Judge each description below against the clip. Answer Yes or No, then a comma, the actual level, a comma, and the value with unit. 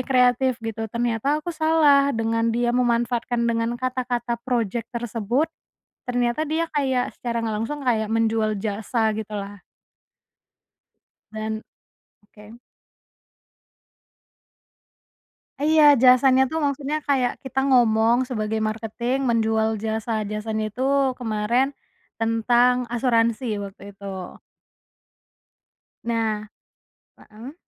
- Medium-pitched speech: No, high, 235 Hz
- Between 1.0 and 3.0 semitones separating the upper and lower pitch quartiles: Yes, narrow, 2.4 semitones